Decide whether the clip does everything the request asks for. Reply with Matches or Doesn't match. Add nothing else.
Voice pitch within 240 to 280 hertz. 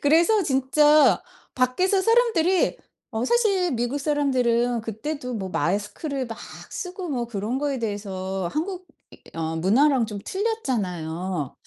Matches